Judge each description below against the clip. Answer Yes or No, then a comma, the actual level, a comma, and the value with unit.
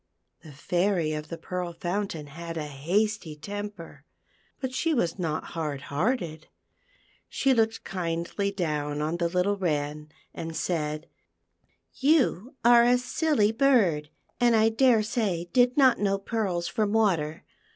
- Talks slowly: No, average, 150 wpm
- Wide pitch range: Yes, wide, 5.8 semitones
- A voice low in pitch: No, medium, 180 Hz